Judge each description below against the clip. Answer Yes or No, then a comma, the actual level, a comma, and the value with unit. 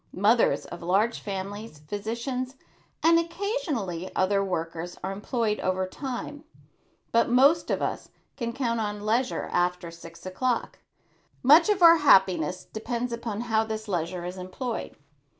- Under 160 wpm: Yes, slow, 135 wpm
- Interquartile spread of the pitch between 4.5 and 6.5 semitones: Yes, average, 5.2 semitones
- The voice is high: Yes, high, 220 Hz